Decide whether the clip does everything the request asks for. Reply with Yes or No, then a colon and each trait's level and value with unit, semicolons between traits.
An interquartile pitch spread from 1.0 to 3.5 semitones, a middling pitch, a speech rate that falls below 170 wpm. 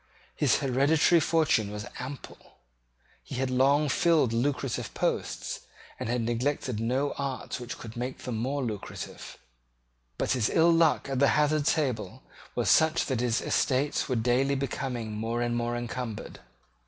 No: average, 3.2 semitones; low, 130 Hz; average, 150 wpm